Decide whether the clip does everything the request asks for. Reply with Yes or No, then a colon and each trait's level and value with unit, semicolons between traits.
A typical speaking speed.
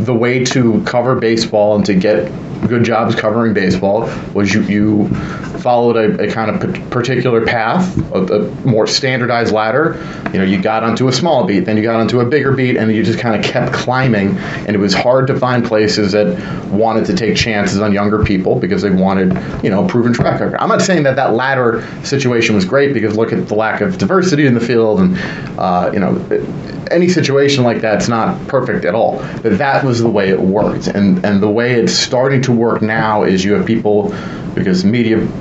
No: fast, 215 wpm